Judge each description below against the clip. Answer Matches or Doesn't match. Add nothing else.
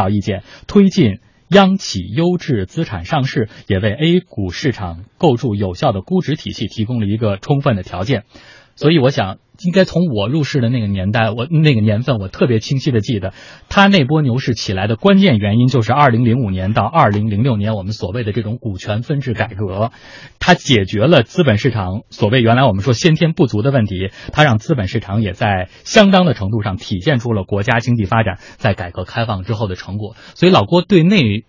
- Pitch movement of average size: Doesn't match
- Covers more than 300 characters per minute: Matches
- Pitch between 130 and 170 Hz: Doesn't match